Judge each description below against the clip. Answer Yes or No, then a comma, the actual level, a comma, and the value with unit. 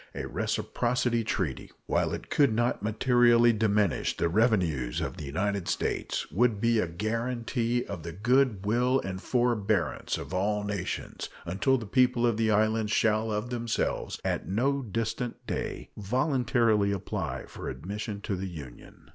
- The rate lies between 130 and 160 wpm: Yes, average, 150 wpm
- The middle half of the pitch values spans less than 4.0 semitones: Yes, average, 3.2 semitones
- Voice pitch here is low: Yes, low, 110 Hz